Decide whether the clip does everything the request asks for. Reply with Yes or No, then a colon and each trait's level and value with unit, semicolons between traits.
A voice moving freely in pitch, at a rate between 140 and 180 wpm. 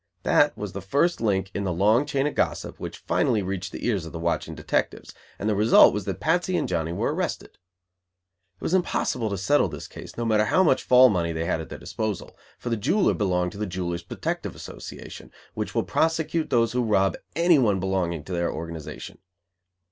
No: wide, 5.9 semitones; fast, 205 wpm